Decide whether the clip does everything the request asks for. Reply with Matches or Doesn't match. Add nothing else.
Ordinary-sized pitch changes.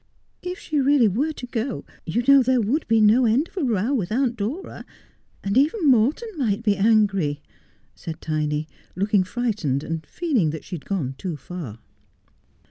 Doesn't match